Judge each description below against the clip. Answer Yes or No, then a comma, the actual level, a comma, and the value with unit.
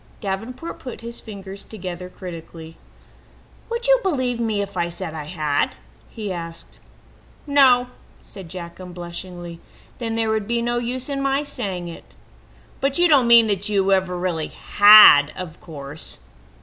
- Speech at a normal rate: Yes, average, 155 wpm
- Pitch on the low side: No, high, 200 Hz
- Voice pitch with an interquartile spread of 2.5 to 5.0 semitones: No, wide, 5.6 semitones